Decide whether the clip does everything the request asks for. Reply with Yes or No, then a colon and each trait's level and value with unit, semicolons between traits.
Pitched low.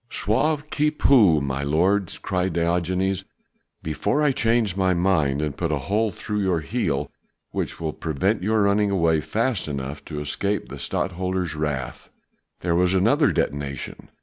Yes: very low, 90 Hz